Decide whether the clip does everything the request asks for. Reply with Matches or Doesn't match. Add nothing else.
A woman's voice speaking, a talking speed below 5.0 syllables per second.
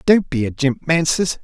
Doesn't match